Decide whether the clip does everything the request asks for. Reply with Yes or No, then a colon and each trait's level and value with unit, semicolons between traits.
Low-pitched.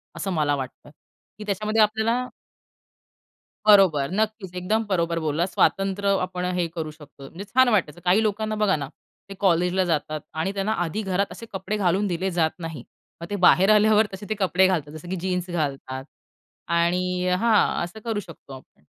No: medium, 185 Hz